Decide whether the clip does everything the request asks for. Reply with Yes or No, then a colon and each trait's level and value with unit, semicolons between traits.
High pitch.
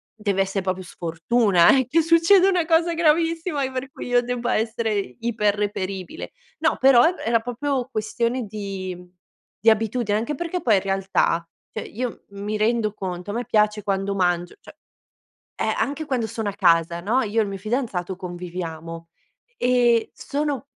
Yes: high, 220 Hz